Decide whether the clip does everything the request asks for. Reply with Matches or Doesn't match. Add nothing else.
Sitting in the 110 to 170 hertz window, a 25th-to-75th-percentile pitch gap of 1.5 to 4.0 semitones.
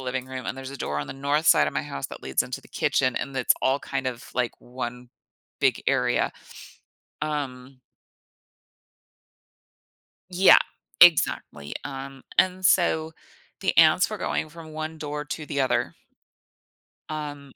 Matches